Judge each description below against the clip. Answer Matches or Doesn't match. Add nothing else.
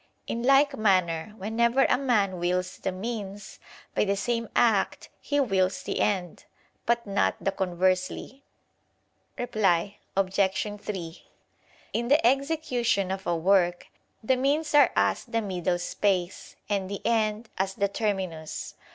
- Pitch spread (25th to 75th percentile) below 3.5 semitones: Doesn't match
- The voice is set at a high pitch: Matches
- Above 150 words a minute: Doesn't match